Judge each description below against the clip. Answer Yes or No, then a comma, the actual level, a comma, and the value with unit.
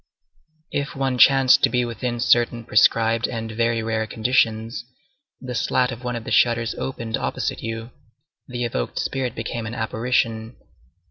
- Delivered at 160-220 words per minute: No, average, 150 wpm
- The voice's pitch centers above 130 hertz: No, low, 115 Hz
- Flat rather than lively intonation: Yes, narrow, 1.7 semitones